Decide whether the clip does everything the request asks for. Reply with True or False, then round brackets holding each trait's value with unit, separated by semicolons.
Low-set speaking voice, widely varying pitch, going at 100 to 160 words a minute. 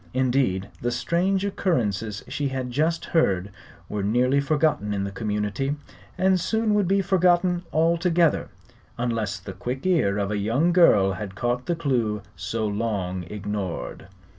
True (125 Hz; 8.4 semitones; 145 wpm)